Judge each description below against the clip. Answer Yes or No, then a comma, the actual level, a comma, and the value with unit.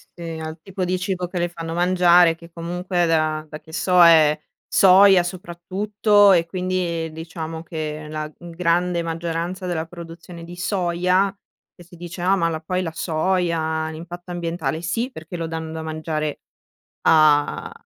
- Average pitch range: No, narrow, 1.9 semitones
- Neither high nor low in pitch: Yes, medium, 170 Hz